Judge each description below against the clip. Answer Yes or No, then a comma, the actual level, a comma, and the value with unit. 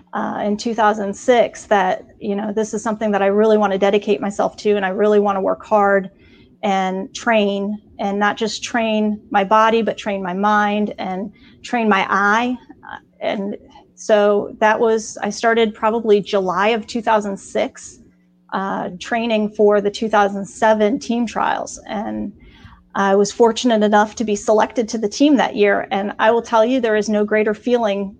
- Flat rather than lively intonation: Yes, narrow, 1.8 semitones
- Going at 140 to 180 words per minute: Yes, average, 170 wpm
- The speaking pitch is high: Yes, high, 210 Hz